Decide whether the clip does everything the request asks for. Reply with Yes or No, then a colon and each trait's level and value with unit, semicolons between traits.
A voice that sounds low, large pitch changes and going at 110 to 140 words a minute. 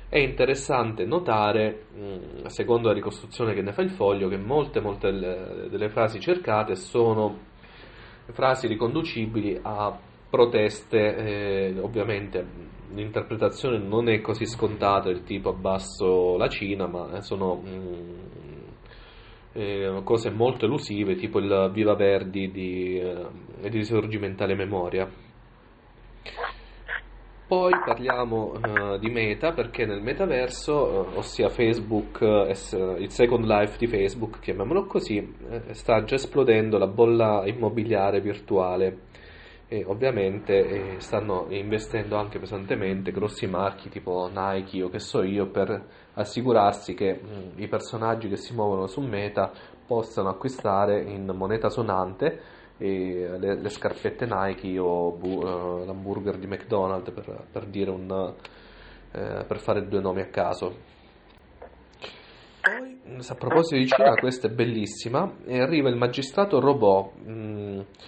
No: low, 105 Hz; average, 3.3 semitones; average, 125 wpm